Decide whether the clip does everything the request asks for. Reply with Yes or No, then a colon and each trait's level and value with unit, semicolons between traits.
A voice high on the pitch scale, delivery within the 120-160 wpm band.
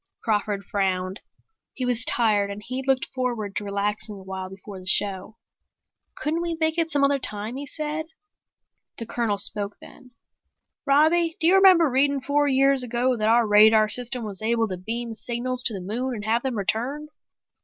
No: high, 235 Hz; average, 180 wpm